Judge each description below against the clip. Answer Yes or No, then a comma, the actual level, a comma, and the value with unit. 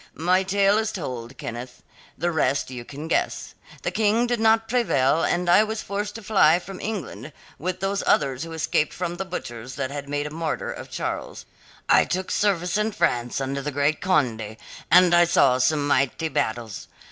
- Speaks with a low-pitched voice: No, medium, 165 Hz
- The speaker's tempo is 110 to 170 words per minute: No, average, 185 wpm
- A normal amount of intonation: No, wide, 6.3 semitones